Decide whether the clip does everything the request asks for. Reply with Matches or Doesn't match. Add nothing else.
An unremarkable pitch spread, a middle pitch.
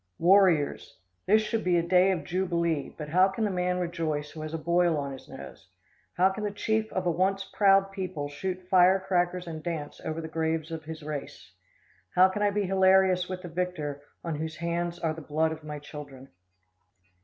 Matches